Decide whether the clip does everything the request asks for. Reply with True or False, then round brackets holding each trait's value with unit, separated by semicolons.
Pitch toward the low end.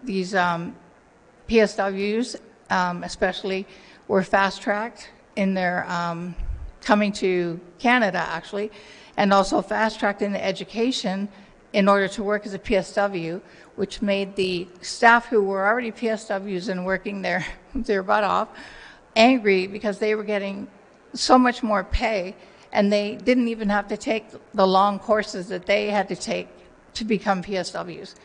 False (200 Hz)